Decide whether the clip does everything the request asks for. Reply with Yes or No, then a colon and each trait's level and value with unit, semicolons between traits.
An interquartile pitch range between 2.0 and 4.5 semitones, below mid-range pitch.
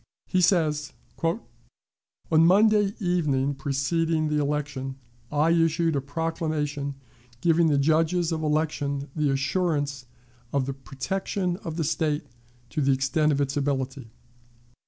No: average, 2.8 semitones; medium, 150 Hz